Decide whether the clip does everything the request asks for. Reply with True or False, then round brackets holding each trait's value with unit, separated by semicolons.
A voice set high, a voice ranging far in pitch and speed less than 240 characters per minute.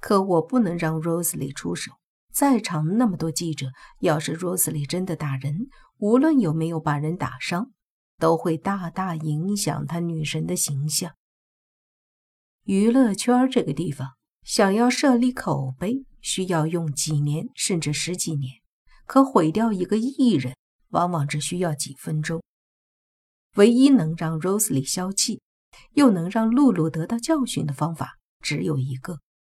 False (170 Hz; 6.2 semitones; 225 characters per minute)